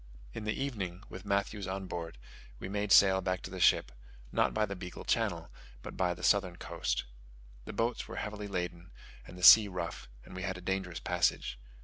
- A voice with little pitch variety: Yes, narrow, 2.3 semitones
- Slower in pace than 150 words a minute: No, average, 200 wpm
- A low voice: Yes, very low, 95 Hz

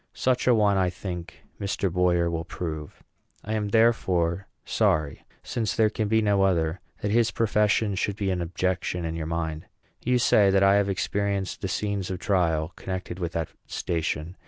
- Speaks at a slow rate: No, average, 180 wpm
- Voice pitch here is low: Yes, very low, 95 Hz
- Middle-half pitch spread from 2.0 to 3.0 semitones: No, average, 3.4 semitones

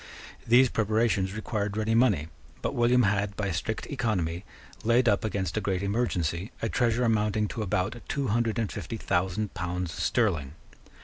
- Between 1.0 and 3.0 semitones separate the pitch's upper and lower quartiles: No, average, 3.4 semitones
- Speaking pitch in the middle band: No, low, 105 Hz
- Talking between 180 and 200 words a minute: No, average, 160 wpm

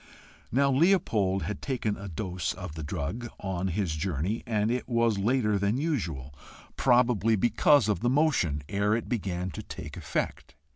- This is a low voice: Yes, low, 105 Hz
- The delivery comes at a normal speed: Yes, average, 160 wpm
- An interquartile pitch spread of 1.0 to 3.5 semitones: No, average, 4.8 semitones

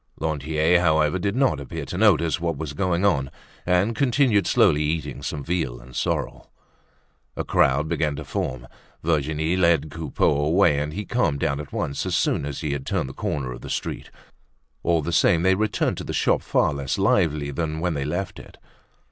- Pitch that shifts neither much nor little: Yes, average, 3.6 semitones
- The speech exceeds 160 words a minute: Yes, average, 190 wpm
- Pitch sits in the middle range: No, very low, 80 Hz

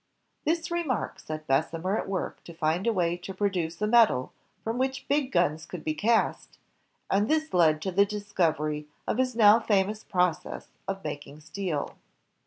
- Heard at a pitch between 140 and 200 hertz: Yes, high, 190 Hz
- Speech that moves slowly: No, average, 170 wpm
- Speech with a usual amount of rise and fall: No, wide, 5.8 semitones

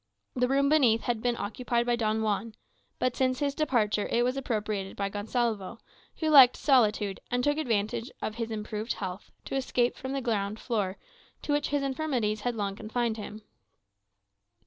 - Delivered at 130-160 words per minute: No, average, 170 wpm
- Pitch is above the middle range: Yes, high, 235 Hz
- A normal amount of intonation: Yes, average, 3.5 semitones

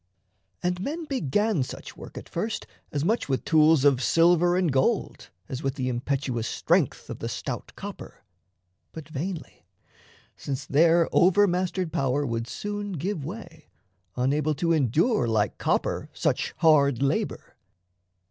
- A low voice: No, medium, 155 Hz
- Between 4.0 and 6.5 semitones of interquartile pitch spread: Yes, average, 4.7 semitones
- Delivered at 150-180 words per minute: No, average, 140 wpm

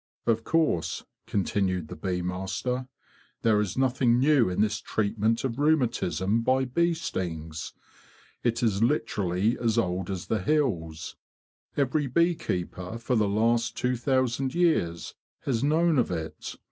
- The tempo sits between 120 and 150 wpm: Yes, average, 145 wpm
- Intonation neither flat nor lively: No, wide, 5.9 semitones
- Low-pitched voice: Yes, low, 115 Hz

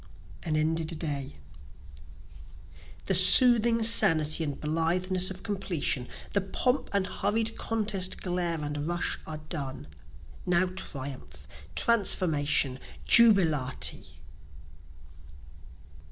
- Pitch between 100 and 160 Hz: No, medium, 175 Hz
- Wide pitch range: No, average, 4.7 semitones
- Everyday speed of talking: No, slow, 90 wpm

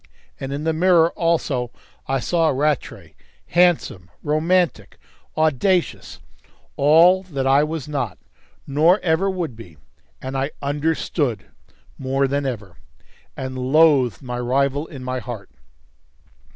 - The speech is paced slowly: Yes, slow, 120 wpm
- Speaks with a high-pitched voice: No, medium, 140 Hz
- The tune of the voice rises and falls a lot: No, average, 4.0 semitones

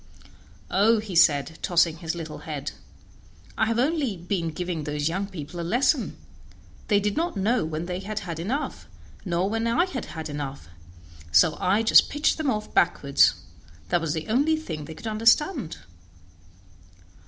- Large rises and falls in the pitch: Yes, wide, 5.9 semitones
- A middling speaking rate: Yes, average, 165 wpm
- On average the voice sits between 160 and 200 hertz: Yes, high, 190 Hz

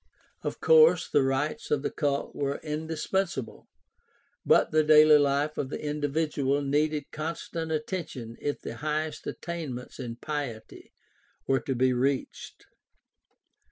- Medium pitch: Yes, medium, 150 Hz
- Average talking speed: No, slow, 125 wpm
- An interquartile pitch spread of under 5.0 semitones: Yes, narrow, 2.4 semitones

